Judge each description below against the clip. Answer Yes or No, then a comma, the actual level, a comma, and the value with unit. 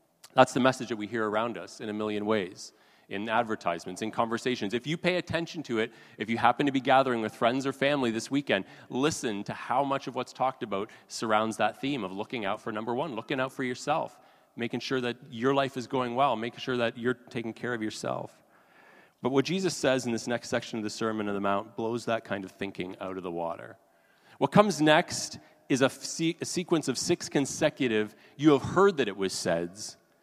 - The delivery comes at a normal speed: No, fast, 220 wpm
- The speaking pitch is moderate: No, low, 125 Hz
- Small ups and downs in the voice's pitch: No, average, 3.8 semitones